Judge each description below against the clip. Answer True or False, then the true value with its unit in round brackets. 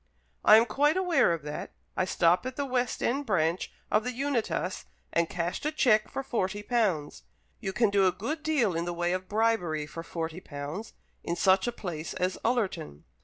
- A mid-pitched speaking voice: False (195 Hz)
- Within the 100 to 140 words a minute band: False (195 wpm)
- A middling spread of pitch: False (6.2 semitones)